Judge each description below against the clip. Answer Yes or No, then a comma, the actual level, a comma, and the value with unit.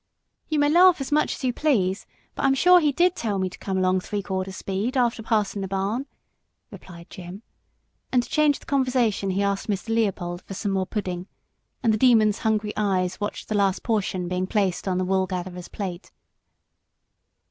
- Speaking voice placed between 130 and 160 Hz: No, high, 200 Hz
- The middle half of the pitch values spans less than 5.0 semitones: Yes, average, 4.5 semitones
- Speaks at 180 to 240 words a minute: Yes, average, 190 wpm